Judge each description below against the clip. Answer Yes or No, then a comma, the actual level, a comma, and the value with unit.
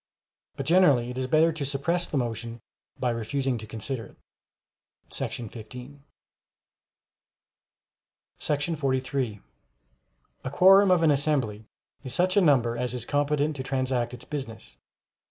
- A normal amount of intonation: Yes, average, 3.9 semitones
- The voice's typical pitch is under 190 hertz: Yes, low, 135 Hz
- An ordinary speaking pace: No, slow, 130 wpm